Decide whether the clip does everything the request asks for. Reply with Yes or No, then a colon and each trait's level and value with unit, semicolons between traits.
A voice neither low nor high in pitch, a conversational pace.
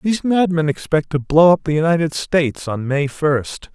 Yes: medium, 160 Hz; average, 190 wpm